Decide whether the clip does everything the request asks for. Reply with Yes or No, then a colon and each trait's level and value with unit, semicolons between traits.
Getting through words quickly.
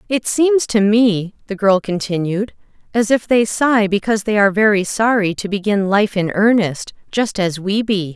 No: average, 175 wpm